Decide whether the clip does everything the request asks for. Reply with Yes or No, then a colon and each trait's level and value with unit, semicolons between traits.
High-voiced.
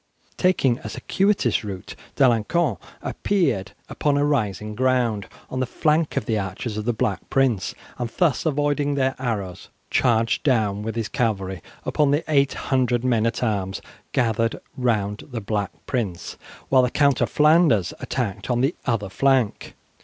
No: low, 120 Hz